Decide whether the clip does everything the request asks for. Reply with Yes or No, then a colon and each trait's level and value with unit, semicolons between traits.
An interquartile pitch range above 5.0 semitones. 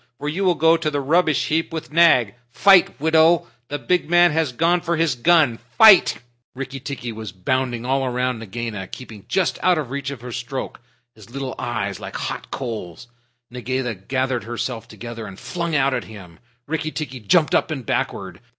Yes: wide, 5.4 semitones